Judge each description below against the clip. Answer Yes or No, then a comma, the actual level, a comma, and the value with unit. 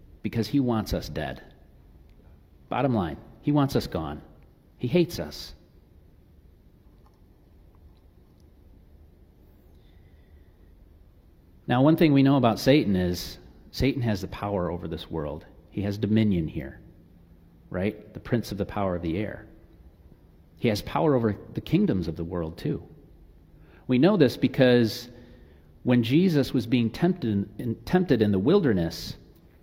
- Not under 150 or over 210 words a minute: No, slow, 135 wpm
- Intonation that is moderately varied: No, wide, 6.1 semitones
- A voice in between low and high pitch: No, very low, 90 Hz